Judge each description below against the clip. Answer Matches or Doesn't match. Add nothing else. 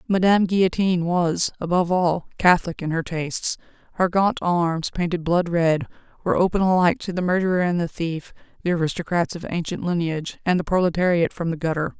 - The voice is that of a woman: Matches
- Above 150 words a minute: Matches